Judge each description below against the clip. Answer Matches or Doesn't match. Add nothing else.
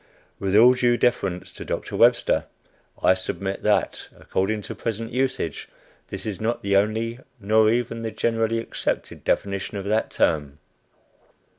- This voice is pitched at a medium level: Doesn't match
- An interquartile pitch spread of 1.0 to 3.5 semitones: Matches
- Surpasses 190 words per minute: Doesn't match